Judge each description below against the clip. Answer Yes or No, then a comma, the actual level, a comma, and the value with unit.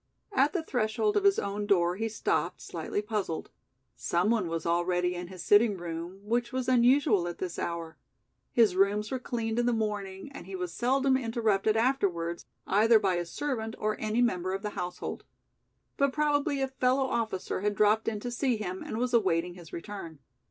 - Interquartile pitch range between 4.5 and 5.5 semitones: Yes, average, 5.1 semitones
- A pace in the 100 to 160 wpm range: No, average, 185 wpm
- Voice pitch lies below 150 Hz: No, high, 210 Hz